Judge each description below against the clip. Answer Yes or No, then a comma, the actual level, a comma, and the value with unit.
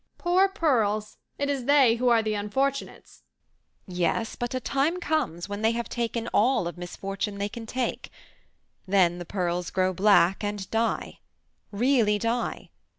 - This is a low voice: No, high, 225 Hz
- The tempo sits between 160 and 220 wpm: No, average, 150 wpm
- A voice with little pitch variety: No, average, 4.5 semitones